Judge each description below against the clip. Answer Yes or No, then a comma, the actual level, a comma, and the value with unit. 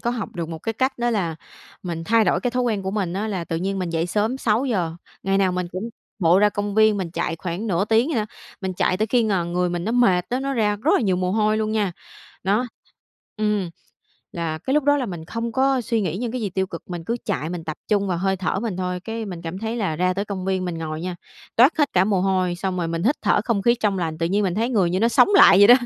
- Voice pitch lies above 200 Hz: No, high, 195 Hz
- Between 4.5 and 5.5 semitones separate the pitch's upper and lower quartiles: No, average, 3.9 semitones